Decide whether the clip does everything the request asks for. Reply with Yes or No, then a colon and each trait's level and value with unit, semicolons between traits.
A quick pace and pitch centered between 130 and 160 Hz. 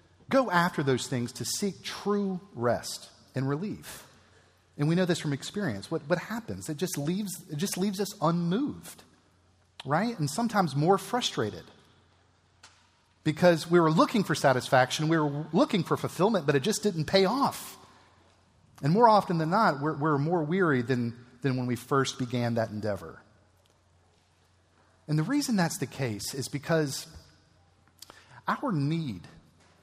No: average, 155 wpm; medium, 140 Hz